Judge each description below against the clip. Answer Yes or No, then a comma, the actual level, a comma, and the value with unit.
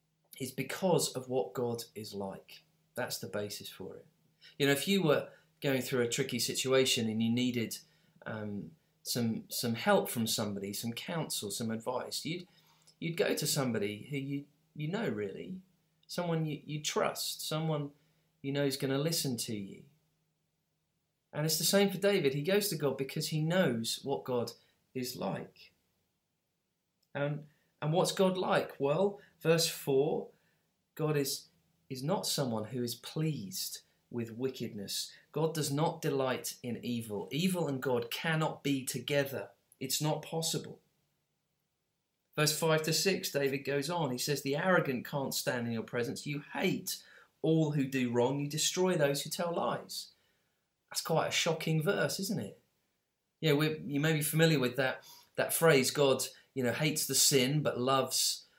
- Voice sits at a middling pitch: Yes, medium, 145 Hz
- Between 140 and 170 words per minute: Yes, average, 165 wpm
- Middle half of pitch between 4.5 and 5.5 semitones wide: No, average, 4.0 semitones